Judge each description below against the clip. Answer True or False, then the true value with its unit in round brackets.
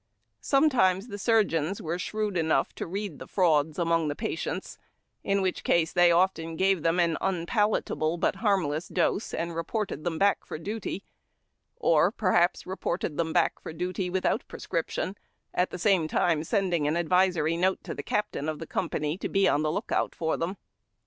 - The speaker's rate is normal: True (175 wpm)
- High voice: False (175 Hz)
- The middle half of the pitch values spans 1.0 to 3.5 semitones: True (3.2 semitones)